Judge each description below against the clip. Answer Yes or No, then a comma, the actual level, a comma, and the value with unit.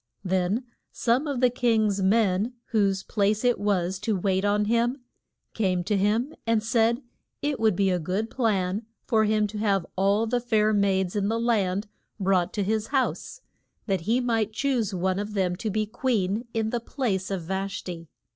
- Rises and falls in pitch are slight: No, average, 3.1 semitones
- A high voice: Yes, high, 210 Hz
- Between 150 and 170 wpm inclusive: No, average, 185 wpm